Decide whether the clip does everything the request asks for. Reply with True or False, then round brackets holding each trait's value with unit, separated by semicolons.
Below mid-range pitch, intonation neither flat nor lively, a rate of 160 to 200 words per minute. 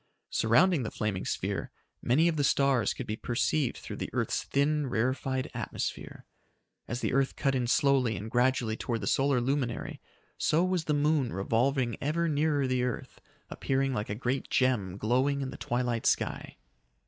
True (130 Hz; 3.2 semitones; 170 wpm)